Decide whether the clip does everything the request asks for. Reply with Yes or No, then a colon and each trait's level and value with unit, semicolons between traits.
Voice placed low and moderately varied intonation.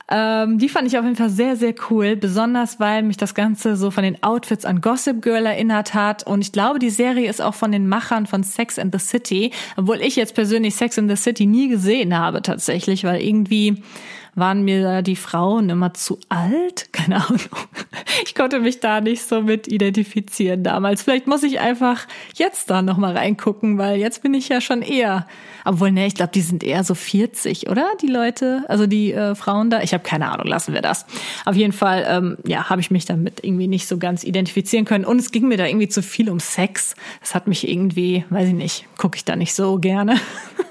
No: high, 210 Hz; average, 3.3 semitones